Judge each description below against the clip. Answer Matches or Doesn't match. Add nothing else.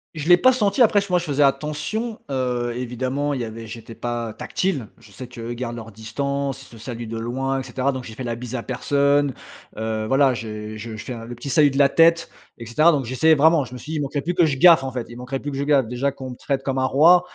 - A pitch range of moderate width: Matches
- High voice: Doesn't match